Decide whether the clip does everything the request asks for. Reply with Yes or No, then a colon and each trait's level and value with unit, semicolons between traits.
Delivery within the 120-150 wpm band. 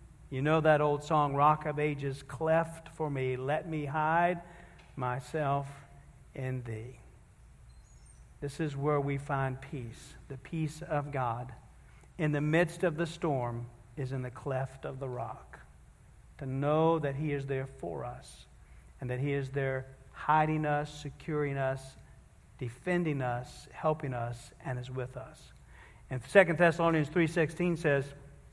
Yes: average, 145 wpm